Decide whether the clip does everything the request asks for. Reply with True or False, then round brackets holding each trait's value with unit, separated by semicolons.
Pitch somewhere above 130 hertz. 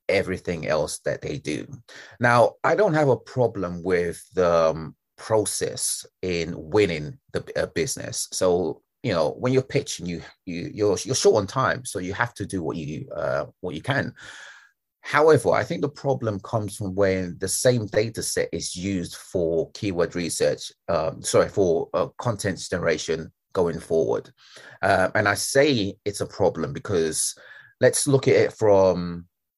False (95 Hz)